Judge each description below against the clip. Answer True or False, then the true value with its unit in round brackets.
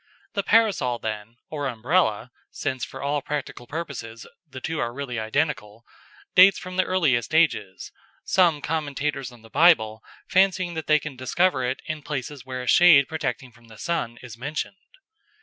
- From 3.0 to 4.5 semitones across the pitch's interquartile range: False (5.2 semitones)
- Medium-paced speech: True (160 wpm)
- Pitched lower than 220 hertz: True (140 Hz)